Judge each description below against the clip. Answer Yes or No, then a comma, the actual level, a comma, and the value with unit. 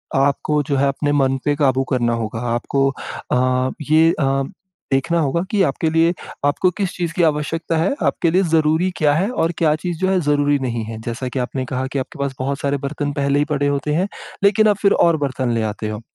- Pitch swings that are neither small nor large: Yes, average, 3.6 semitones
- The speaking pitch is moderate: Yes, medium, 145 Hz